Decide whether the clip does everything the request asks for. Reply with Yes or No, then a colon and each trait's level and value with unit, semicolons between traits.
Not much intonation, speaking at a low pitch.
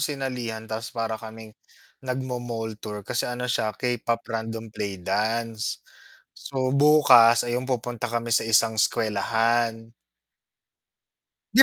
Yes: narrow, 1.7 semitones; low, 115 Hz